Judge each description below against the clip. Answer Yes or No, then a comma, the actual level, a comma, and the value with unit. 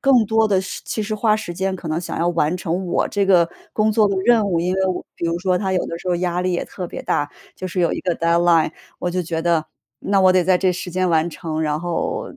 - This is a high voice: No, medium, 180 Hz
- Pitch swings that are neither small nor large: No, narrow, 2.3 semitones